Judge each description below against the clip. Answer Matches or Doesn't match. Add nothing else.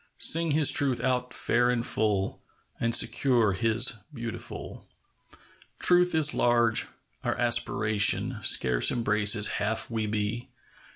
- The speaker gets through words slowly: Matches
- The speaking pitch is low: Matches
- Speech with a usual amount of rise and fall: Matches